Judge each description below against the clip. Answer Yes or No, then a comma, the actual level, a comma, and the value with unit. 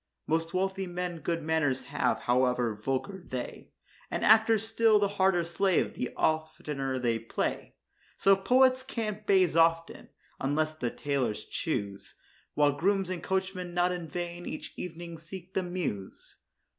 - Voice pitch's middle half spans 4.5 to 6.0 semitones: Yes, average, 4.8 semitones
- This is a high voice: No, medium, 170 Hz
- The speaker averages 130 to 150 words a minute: Yes, average, 145 wpm